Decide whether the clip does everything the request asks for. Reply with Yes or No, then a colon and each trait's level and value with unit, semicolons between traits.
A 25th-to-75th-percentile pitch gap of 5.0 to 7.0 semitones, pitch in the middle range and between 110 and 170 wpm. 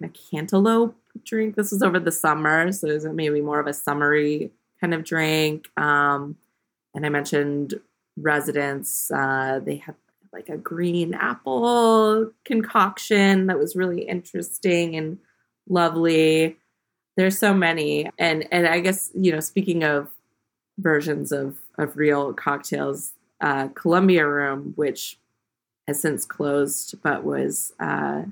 No: average, 4.2 semitones; medium, 155 Hz; slow, 135 wpm